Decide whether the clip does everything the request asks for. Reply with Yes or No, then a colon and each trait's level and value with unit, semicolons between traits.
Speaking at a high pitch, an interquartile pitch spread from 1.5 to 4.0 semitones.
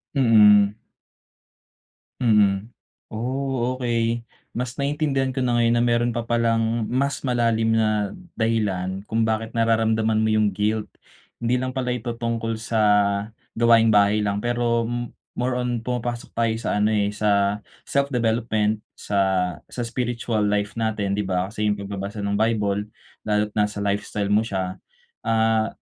No: low, 110 Hz; narrow, 2.4 semitones